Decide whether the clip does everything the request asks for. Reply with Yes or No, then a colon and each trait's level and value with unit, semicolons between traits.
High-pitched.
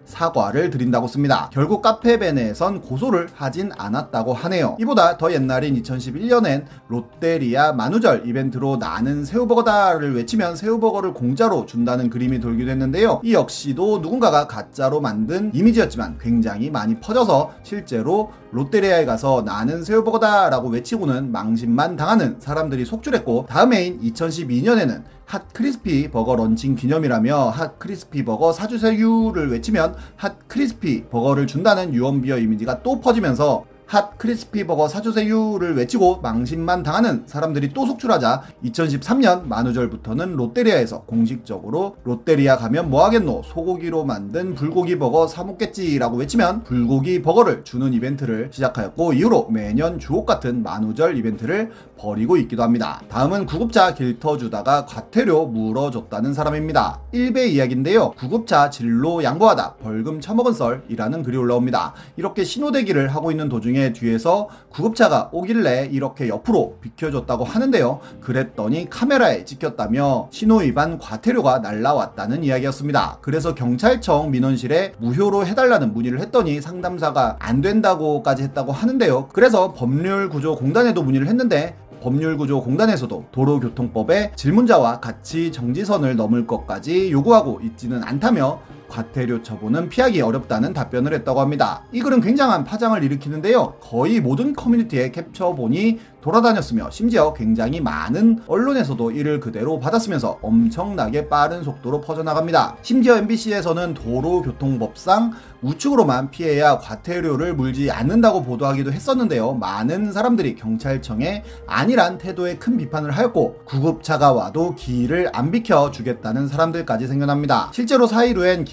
No: medium, 155 Hz